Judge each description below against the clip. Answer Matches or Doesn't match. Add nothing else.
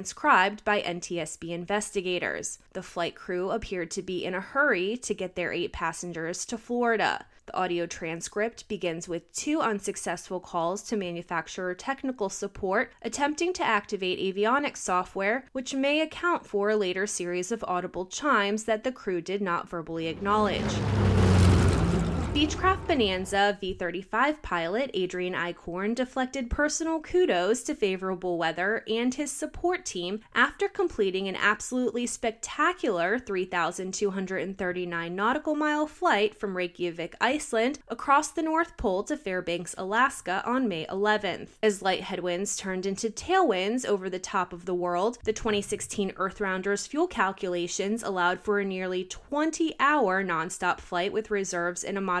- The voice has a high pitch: Matches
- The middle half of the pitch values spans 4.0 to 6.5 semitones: Matches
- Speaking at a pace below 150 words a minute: Matches